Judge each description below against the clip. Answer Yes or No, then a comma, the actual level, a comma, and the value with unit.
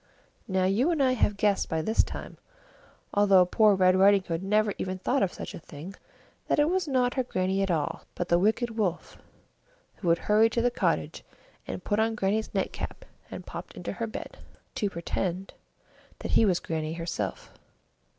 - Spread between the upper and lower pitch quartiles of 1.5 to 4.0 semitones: Yes, average, 3.6 semitones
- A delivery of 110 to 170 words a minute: No, average, 185 wpm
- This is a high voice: Yes, high, 195 Hz